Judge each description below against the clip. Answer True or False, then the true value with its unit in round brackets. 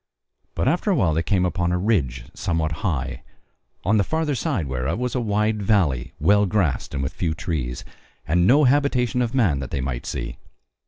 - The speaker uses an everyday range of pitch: False (8.2 semitones)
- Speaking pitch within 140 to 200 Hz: False (90 Hz)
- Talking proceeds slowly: False (195 wpm)